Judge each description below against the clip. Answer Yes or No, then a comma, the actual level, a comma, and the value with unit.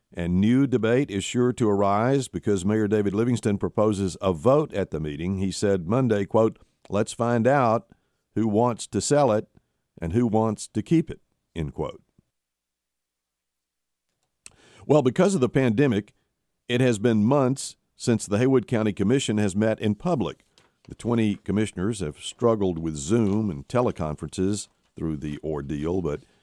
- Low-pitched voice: Yes, low, 105 Hz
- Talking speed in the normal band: Yes, average, 155 wpm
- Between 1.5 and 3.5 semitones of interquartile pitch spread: No, average, 5.3 semitones